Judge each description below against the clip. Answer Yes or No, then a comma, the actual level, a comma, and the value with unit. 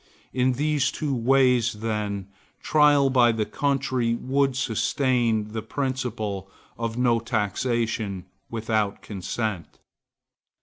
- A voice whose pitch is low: Yes, low, 120 Hz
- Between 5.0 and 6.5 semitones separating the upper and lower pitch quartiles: No, average, 3.3 semitones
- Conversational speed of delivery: No, slow, 100 wpm